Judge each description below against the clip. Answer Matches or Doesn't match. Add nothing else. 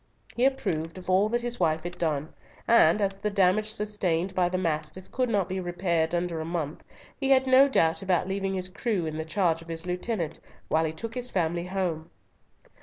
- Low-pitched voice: Doesn't match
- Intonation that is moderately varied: Matches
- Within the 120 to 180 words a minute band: Doesn't match